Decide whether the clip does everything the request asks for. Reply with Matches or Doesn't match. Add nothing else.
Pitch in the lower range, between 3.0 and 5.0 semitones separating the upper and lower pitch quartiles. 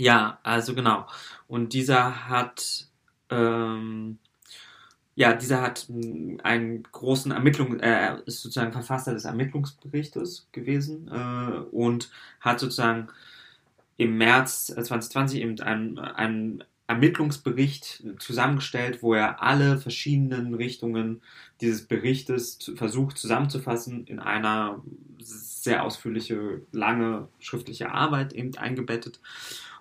Doesn't match